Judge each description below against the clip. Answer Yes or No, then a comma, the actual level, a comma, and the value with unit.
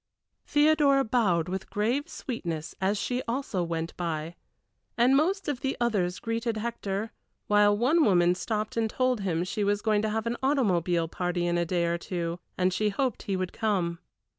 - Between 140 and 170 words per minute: No, average, 180 wpm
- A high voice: Yes, high, 205 Hz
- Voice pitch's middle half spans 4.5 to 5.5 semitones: Yes, average, 5.2 semitones